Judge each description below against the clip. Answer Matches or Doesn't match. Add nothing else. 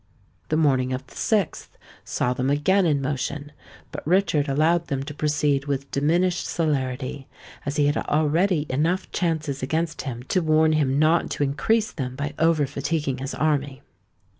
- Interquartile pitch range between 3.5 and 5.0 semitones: Doesn't match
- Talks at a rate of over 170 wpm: Doesn't match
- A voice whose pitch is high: Doesn't match